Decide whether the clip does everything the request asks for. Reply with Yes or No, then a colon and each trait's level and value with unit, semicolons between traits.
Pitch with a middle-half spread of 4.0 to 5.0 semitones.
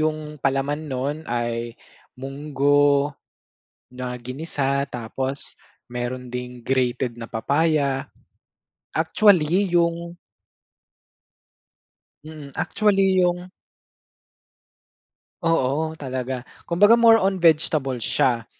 Yes: average, 4.5 semitones